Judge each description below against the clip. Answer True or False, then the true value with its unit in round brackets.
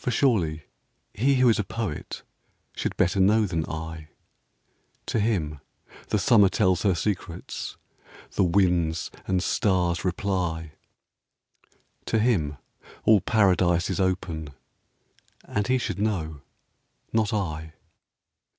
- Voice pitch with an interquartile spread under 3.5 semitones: False (4.5 semitones)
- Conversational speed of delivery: False (125 wpm)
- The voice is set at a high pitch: False (95 Hz)